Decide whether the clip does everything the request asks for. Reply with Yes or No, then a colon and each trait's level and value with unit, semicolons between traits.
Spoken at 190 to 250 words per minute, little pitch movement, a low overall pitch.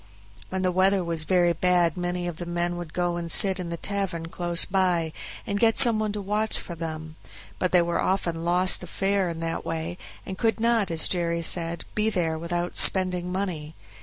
No: average, 200 wpm; narrow, 2.1 semitones; medium, 175 Hz